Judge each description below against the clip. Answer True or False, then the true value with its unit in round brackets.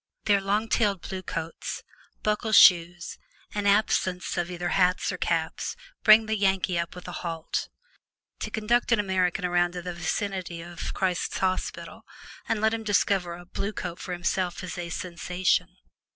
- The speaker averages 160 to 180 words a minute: True (165 wpm)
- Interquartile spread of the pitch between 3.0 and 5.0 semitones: False (2.5 semitones)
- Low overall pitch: False (185 Hz)